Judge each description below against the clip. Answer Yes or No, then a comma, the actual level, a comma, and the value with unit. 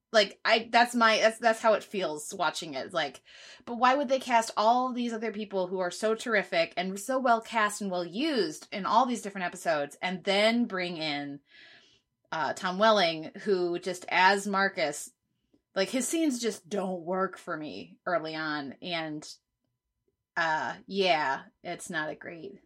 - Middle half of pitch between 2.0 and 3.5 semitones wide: No, average, 4.4 semitones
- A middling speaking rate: Yes, average, 170 wpm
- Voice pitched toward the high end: Yes, high, 200 Hz